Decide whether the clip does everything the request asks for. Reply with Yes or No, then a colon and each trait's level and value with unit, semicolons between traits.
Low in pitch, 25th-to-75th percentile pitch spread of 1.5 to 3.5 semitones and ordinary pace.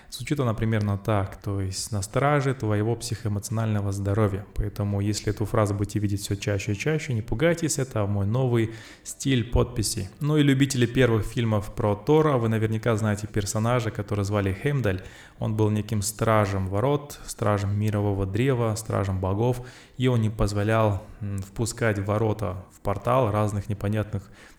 Yes: low, 110 Hz; average, 2.8 semitones; average, 150 wpm